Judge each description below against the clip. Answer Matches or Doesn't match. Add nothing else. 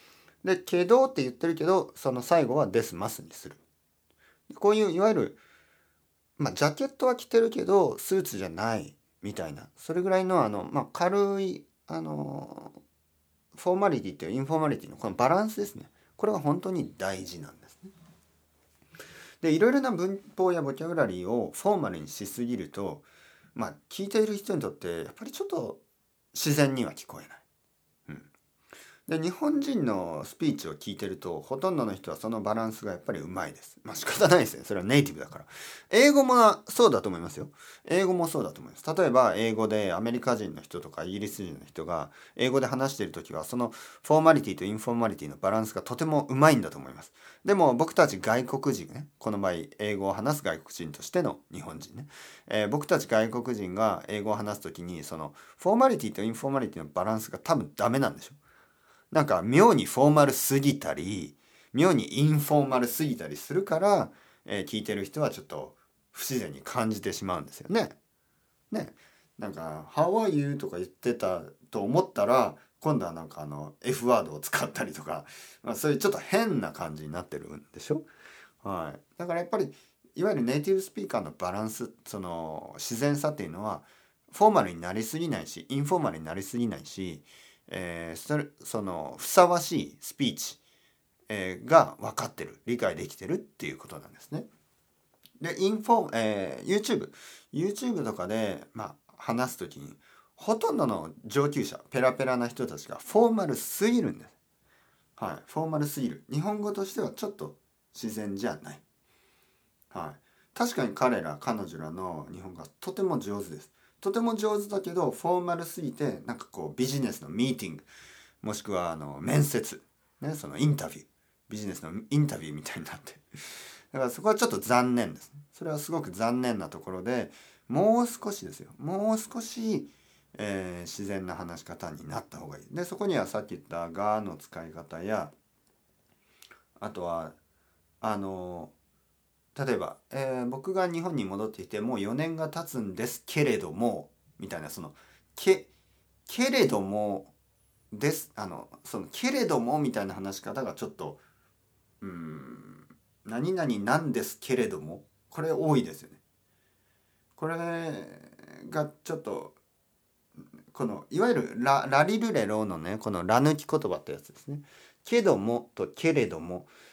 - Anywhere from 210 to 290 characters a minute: Doesn't match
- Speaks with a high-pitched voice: Doesn't match